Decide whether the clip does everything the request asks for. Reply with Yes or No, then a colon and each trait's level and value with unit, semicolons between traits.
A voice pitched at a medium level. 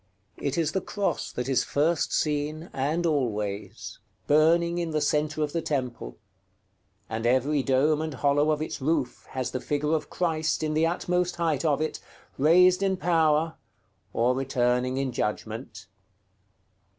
Yes: medium, 150 Hz